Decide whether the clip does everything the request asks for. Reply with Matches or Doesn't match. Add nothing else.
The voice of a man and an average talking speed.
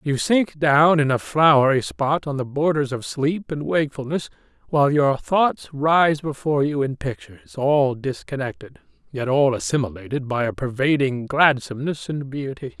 Matches